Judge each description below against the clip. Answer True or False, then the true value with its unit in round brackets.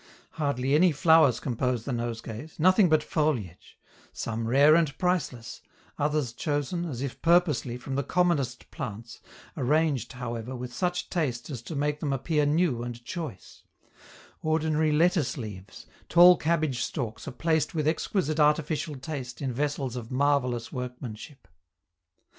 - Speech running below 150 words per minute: True (140 wpm)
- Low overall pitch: False (145 Hz)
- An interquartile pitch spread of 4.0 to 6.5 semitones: True (4.4 semitones)